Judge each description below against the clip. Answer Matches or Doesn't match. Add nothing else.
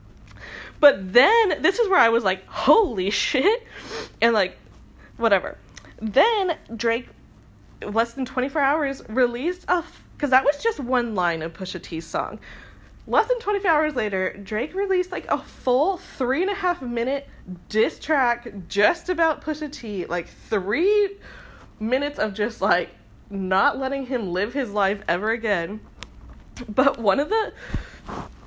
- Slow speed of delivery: Doesn't match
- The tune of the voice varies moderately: Doesn't match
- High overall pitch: Matches